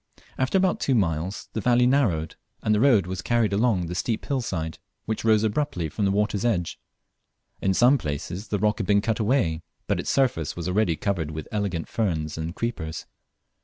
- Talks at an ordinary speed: Yes, average, 195 wpm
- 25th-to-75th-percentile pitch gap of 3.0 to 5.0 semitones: No, wide, 5.6 semitones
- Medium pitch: No, low, 100 Hz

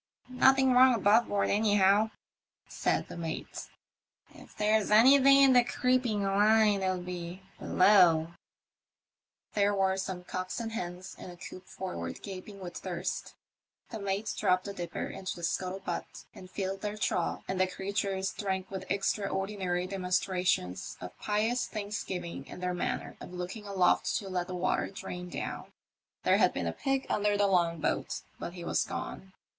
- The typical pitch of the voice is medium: No, high, 195 Hz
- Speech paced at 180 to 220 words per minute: No, average, 165 wpm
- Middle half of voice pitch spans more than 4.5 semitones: No, narrow, 2.6 semitones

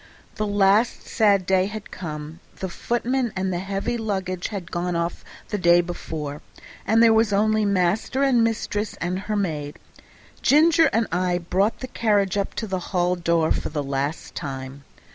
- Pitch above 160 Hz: Yes, high, 190 Hz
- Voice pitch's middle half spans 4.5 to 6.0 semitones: No, average, 4.0 semitones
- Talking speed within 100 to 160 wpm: No, average, 170 wpm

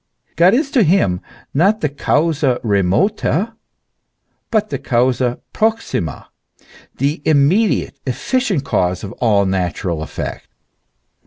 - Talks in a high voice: No, medium, 145 Hz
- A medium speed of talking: No, slow, 105 wpm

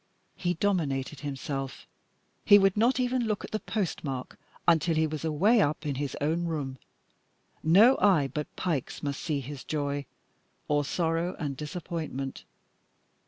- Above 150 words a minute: No, average, 145 wpm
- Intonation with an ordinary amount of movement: Yes, average, 4.3 semitones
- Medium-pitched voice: Yes, medium, 155 Hz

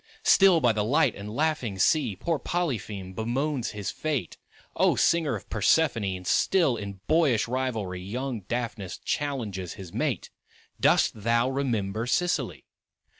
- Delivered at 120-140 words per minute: Yes, slow, 135 wpm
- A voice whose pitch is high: No, low, 120 Hz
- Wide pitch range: Yes, wide, 6.4 semitones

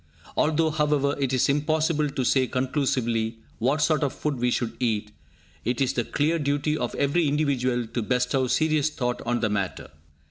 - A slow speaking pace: No, average, 175 wpm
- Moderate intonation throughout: Yes, average, 3.5 semitones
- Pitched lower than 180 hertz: Yes, low, 135 Hz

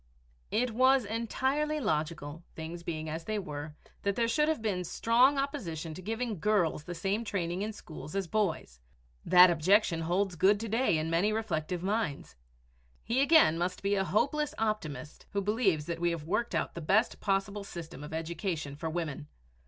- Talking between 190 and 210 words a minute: No, average, 175 wpm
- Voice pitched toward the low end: No, high, 190 Hz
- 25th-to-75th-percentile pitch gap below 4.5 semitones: No, average, 5.3 semitones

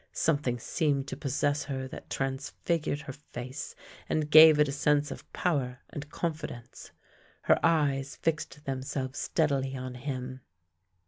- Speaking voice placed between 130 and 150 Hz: Yes, medium, 140 Hz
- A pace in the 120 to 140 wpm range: Yes, slow, 135 wpm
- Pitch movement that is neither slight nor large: No, narrow, 2.3 semitones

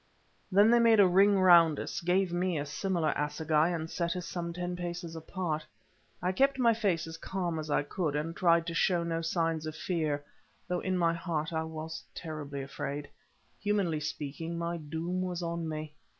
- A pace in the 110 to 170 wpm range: No, average, 190 wpm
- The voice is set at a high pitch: No, medium, 170 Hz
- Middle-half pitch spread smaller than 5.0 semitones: Yes, narrow, 2.4 semitones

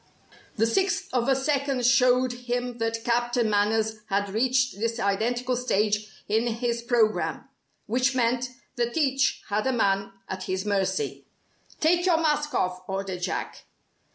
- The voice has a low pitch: No, high, 240 Hz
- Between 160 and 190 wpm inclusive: No, average, 145 wpm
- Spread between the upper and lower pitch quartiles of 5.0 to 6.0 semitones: No, average, 3.4 semitones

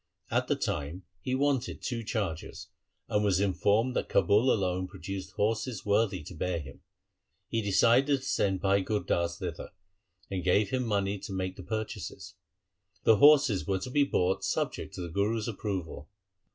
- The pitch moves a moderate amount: Yes, average, 3.6 semitones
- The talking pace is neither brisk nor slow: Yes, average, 165 wpm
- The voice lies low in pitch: Yes, low, 100 Hz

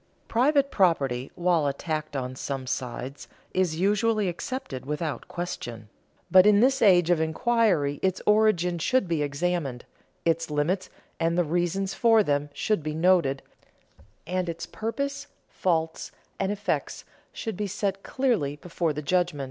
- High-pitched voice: No, medium, 175 Hz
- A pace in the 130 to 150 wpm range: Yes, average, 140 wpm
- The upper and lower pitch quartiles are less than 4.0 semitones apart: No, average, 5.2 semitones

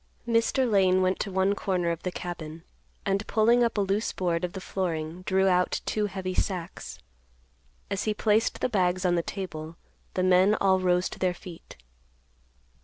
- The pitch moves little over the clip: Yes, narrow, 2.1 semitones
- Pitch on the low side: No, medium, 185 Hz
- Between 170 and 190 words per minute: Yes, average, 180 wpm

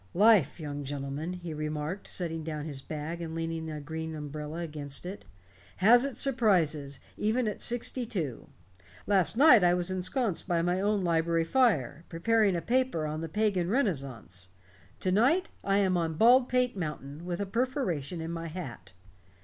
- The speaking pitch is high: No, medium, 170 Hz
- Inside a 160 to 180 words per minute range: Yes, average, 165 wpm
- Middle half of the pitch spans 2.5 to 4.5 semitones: No, wide, 5.4 semitones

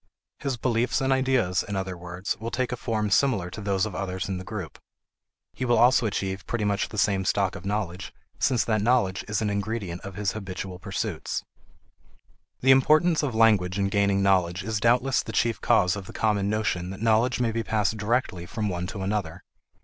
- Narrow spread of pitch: No, average, 3.5 semitones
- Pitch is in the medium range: No, low, 105 Hz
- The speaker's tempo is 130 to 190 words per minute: No, average, 200 wpm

